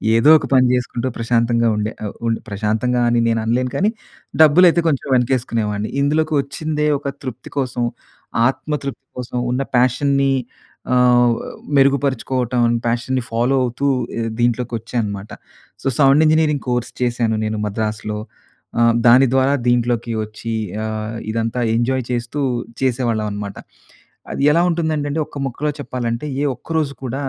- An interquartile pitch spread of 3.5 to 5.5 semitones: No, average, 3.1 semitones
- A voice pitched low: Yes, low, 125 Hz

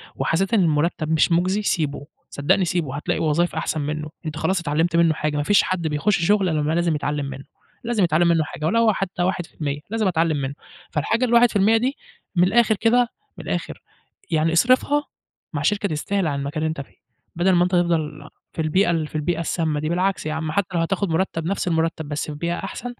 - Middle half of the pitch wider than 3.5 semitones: Yes, average, 4.0 semitones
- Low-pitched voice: No, medium, 170 Hz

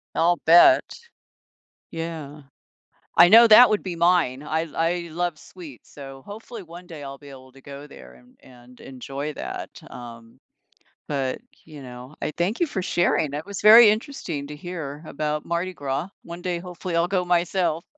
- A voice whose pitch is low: No, medium, 165 Hz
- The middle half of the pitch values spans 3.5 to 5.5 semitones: Yes, average, 4.1 semitones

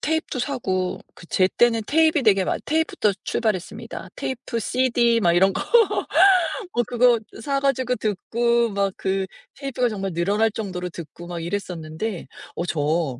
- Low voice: No, high, 215 Hz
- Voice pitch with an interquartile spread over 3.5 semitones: Yes, average, 5.2 semitones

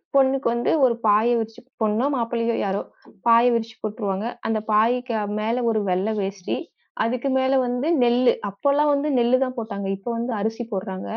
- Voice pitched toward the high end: Yes, high, 230 Hz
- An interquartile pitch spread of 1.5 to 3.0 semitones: Yes, average, 2.7 semitones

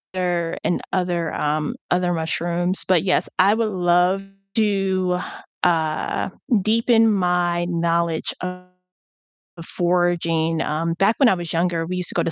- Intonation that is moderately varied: No, narrow, 1.8 semitones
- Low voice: No, medium, 175 Hz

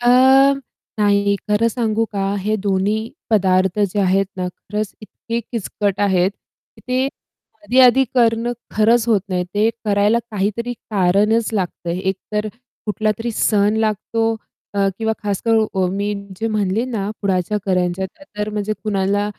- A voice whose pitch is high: Yes, high, 210 Hz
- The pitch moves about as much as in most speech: No, narrow, 2.3 semitones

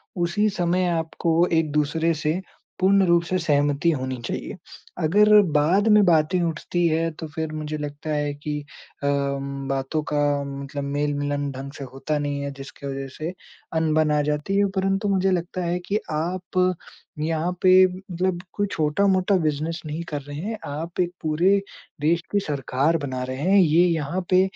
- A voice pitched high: No, medium, 160 Hz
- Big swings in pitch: No, average, 3.8 semitones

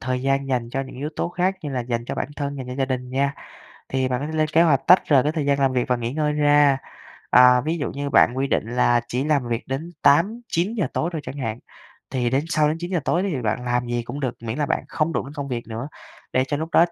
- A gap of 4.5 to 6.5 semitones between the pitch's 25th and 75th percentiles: No, average, 3.3 semitones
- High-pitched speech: No, low, 135 Hz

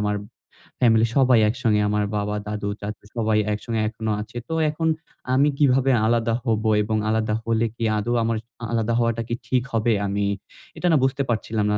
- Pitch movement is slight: Yes, narrow, 2.1 semitones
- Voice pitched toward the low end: Yes, low, 115 Hz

